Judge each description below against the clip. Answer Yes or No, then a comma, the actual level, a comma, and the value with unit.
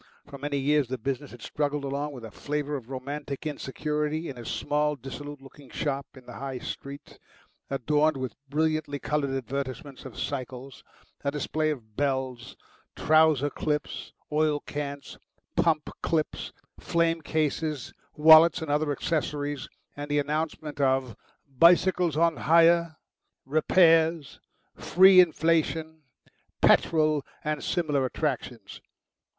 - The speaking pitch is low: No, medium, 145 Hz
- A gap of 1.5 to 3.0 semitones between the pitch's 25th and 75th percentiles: Yes, narrow, 2.4 semitones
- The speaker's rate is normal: No, slow, 125 wpm